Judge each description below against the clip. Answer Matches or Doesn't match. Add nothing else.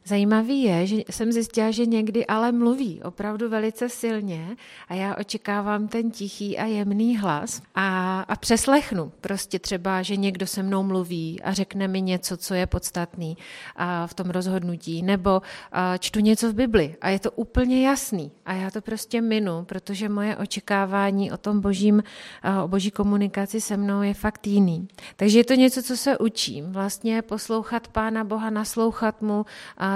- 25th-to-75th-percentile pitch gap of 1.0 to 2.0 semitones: Doesn't match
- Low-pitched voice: Doesn't match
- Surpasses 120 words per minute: Matches